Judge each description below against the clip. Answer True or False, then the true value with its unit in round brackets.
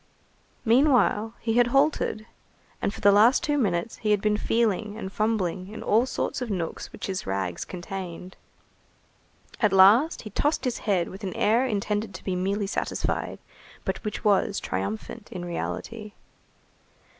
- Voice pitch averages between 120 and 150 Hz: False (210 Hz)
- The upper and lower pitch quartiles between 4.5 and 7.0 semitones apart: False (3.3 semitones)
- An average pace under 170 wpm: True (155 wpm)